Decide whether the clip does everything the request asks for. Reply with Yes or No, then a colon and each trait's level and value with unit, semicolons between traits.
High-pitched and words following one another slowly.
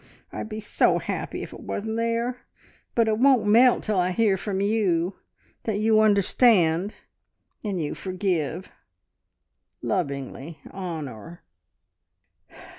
Yes: high, 200 Hz; slow, 115 wpm